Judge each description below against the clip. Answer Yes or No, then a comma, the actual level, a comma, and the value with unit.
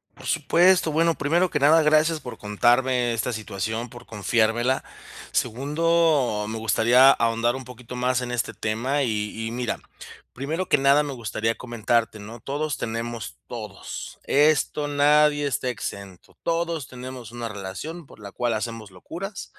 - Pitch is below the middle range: Yes, low, 125 Hz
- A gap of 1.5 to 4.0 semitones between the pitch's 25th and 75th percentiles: No, average, 4.6 semitones